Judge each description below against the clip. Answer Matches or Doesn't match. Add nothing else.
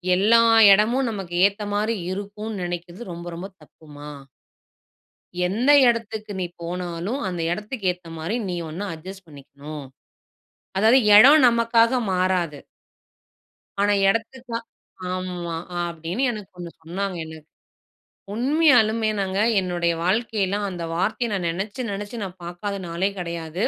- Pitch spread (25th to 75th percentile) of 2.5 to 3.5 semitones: Doesn't match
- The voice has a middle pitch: Doesn't match